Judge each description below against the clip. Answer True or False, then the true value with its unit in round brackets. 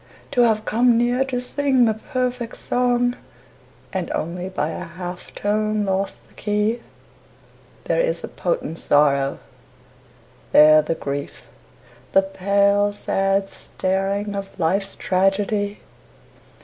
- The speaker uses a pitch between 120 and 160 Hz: False (200 Hz)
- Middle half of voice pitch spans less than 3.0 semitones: False (4.0 semitones)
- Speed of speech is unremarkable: False (120 wpm)